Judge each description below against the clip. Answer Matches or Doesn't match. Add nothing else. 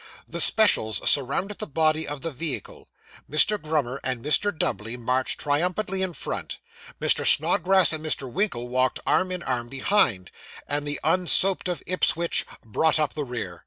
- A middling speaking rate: Matches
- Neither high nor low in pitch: Matches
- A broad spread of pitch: Matches